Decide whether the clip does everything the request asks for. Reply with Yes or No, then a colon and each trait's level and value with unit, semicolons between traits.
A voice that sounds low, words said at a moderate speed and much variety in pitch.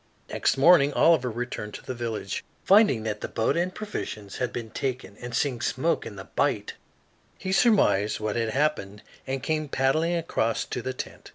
Yes: low, 130 Hz; average, 180 wpm; wide, 6.0 semitones